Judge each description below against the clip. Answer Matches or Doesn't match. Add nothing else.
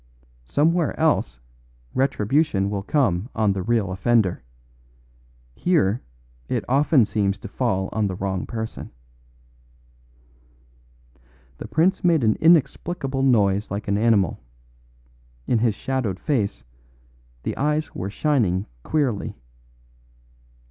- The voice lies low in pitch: Matches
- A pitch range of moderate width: Doesn't match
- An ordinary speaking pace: Doesn't match